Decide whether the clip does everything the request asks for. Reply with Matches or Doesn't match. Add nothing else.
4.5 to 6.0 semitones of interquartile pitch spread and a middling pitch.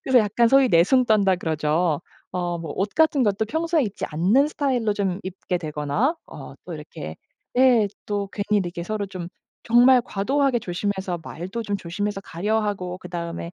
Doesn't match